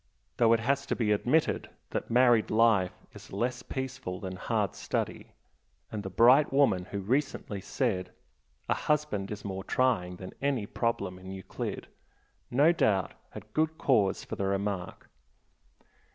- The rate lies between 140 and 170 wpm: Yes, average, 150 wpm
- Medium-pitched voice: No, low, 110 Hz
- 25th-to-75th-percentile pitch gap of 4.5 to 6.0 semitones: Yes, average, 5.1 semitones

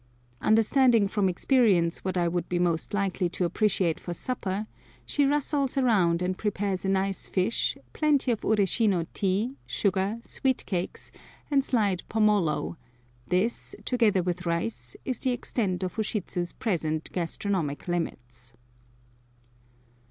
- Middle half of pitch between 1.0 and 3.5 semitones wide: No, average, 4.2 semitones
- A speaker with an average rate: No, slow, 130 wpm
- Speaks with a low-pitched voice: No, high, 195 Hz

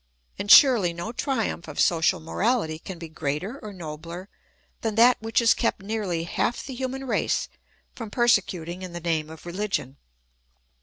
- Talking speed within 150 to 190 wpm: Yes, average, 160 wpm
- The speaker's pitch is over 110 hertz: Yes, high, 190 Hz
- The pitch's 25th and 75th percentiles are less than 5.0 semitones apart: No, wide, 5.6 semitones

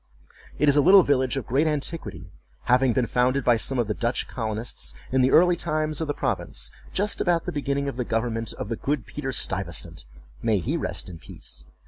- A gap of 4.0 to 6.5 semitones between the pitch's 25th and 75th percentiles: Yes, average, 4.5 semitones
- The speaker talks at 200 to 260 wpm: Yes, fast, 205 wpm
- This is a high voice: No, low, 130 Hz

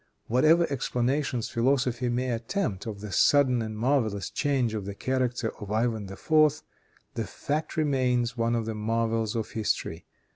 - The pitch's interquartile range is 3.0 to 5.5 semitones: Yes, average, 3.3 semitones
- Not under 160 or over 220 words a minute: No, average, 150 wpm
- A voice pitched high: No, low, 120 Hz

